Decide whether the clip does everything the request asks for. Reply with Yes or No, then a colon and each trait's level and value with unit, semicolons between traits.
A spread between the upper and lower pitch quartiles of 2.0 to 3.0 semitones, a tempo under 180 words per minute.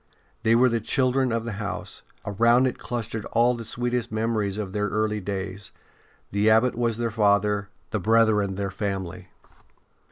Yes: narrow, 2.4 semitones; average, 160 wpm